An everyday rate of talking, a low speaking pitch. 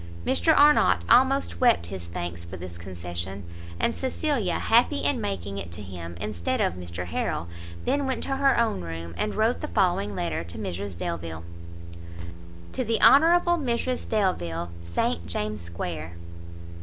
Yes: average, 155 wpm; very low, 95 Hz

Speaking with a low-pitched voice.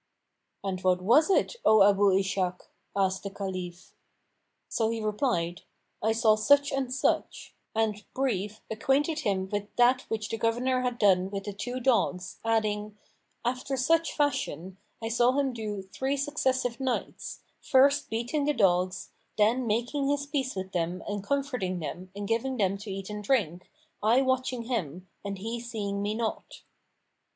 No: high, 220 Hz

